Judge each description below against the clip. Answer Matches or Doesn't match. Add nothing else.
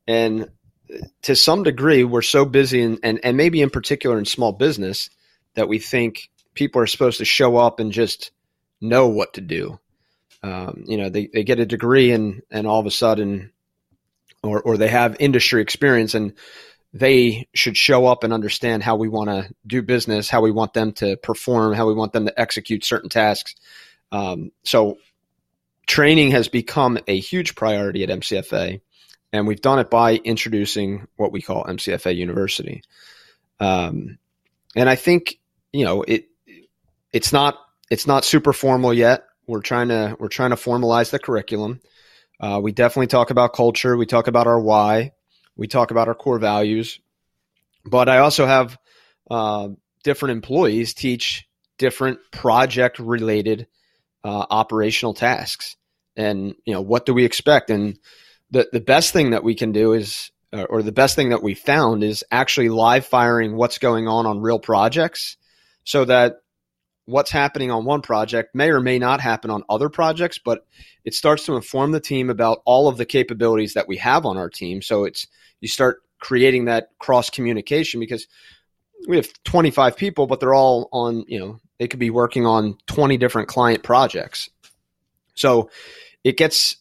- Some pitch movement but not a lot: Matches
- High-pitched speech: Doesn't match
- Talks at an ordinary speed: Matches